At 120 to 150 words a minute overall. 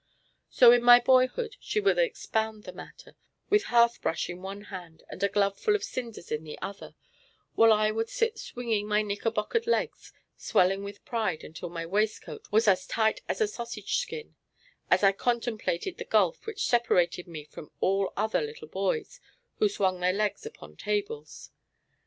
No: average, 170 wpm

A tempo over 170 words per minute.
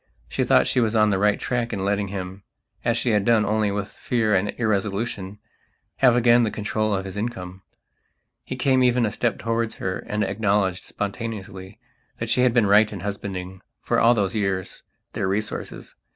Yes: average, 180 wpm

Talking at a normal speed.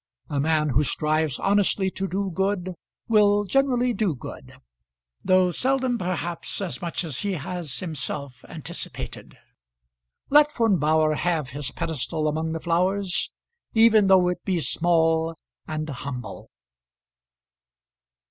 No: slow, 125 wpm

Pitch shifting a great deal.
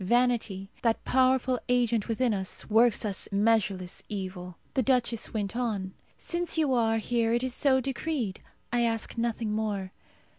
No: average, 3.4 semitones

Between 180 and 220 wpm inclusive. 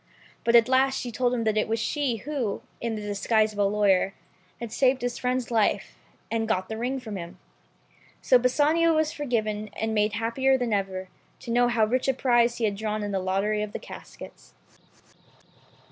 Yes: average, 195 wpm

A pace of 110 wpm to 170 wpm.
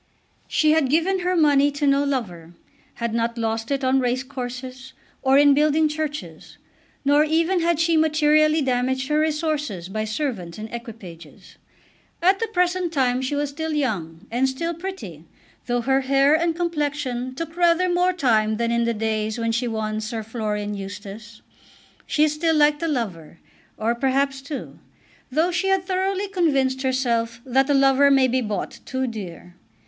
Yes: average, 165 wpm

